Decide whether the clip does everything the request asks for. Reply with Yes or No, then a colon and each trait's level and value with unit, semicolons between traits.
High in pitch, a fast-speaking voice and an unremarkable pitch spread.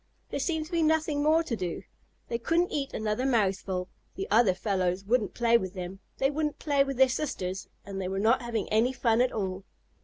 No: high, 235 Hz; fast, 210 wpm; wide, 6.6 semitones